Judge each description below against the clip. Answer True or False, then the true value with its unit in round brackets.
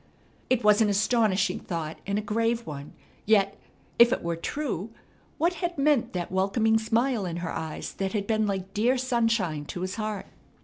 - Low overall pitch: False (210 Hz)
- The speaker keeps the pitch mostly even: False (3.8 semitones)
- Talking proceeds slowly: False (180 wpm)